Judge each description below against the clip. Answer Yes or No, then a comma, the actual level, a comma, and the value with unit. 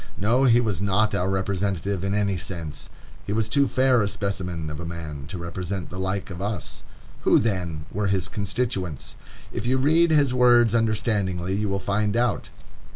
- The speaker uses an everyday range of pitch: Yes, average, 3.8 semitones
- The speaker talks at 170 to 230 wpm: Yes, average, 180 wpm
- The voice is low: Yes, low, 100 Hz